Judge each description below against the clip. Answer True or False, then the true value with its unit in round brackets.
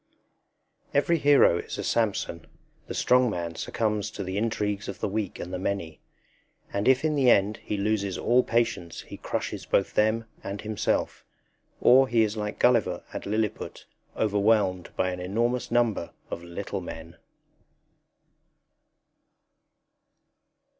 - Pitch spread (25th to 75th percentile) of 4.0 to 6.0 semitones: False (3.5 semitones)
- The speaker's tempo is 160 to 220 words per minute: False (140 wpm)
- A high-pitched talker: False (105 Hz)